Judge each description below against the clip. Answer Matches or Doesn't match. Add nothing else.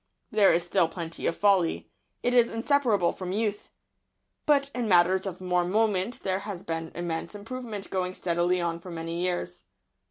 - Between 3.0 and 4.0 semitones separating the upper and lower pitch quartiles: Matches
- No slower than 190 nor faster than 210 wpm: Doesn't match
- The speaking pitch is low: Doesn't match